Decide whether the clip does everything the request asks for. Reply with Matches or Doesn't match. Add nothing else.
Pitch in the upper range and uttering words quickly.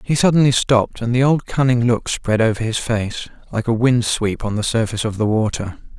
Doesn't match